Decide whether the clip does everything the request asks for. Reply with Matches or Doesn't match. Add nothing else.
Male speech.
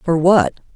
Doesn't match